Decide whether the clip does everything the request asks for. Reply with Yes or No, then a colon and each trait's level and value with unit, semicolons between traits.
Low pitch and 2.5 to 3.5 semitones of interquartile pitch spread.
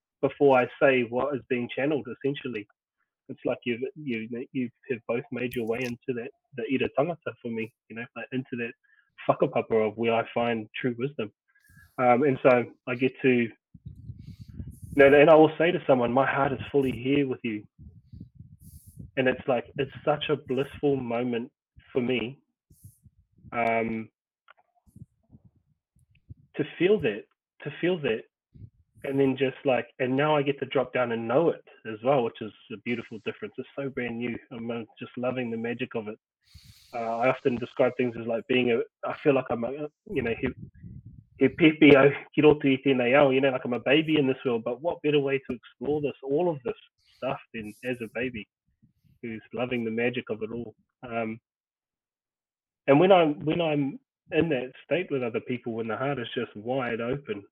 Yes: low, 125 Hz; average, 3.2 semitones